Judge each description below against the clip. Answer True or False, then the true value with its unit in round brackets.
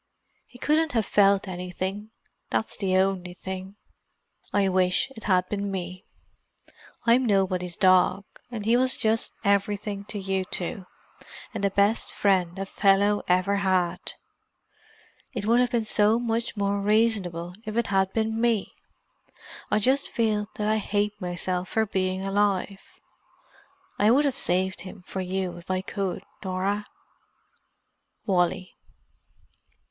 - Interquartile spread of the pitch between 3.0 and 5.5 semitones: False (2.5 semitones)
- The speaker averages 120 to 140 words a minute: True (135 wpm)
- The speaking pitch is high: True (200 Hz)